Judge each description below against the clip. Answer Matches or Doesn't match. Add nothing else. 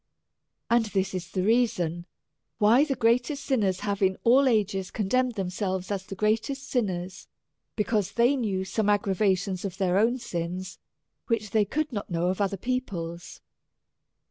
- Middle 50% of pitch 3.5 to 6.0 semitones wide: Matches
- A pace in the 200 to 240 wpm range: Doesn't match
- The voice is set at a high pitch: Matches